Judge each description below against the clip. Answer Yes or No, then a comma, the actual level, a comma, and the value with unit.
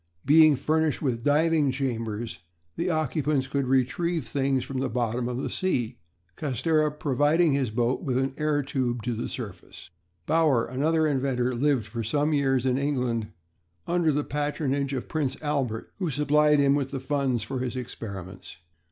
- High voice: No, low, 135 Hz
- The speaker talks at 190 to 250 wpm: No, average, 160 wpm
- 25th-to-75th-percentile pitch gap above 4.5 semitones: No, average, 3.3 semitones